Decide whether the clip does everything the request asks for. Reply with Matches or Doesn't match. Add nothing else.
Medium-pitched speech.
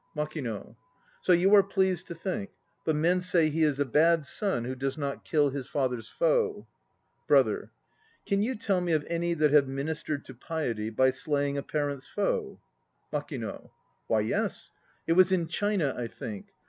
Matches